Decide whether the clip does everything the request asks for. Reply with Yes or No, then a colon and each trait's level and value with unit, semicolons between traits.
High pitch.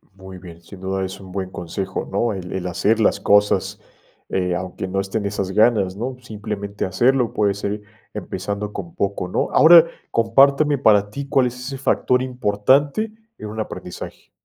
No: low, 105 Hz